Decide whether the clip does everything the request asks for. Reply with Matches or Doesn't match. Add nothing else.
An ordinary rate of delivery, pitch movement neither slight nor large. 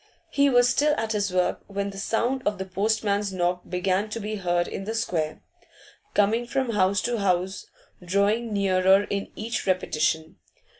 Matches